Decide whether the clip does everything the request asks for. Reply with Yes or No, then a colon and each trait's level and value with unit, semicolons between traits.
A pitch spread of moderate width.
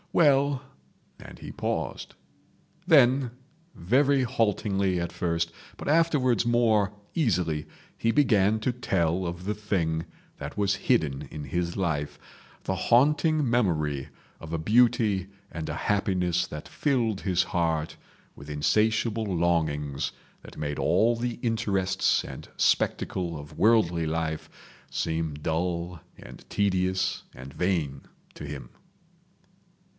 No: wide, 6.1 semitones